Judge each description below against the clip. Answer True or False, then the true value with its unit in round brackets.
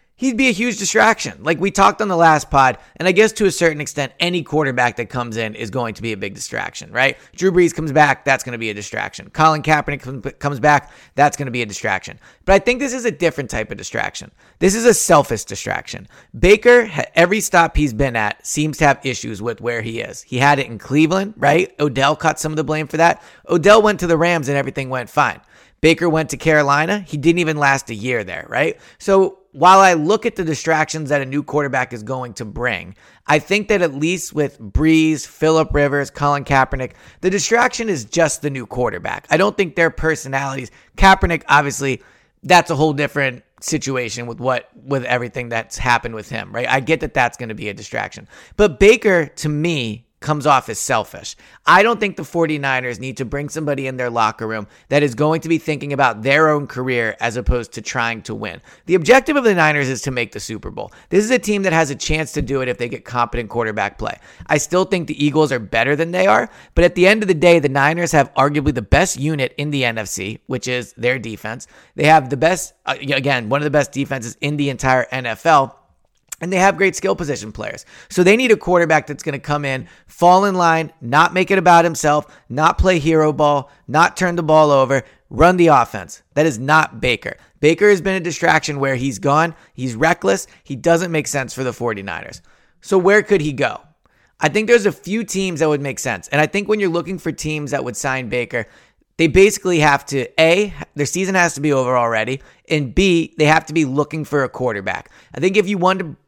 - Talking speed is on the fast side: True (225 wpm)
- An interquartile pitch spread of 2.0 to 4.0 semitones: False (4.9 semitones)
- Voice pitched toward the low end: False (150 Hz)